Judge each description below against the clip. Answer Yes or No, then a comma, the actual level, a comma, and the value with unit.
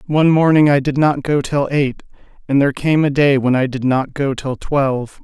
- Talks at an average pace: No, fast, 230 wpm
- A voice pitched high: No, medium, 140 Hz